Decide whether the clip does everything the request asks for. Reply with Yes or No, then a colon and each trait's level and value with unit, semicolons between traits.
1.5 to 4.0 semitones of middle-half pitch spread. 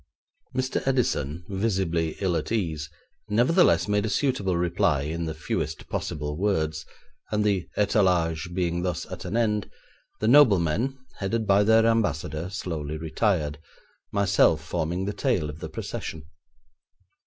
No: average, 4.7 semitones